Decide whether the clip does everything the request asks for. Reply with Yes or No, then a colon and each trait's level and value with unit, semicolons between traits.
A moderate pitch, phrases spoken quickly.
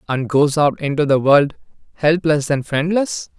No: medium, 150 Hz; average, 160 wpm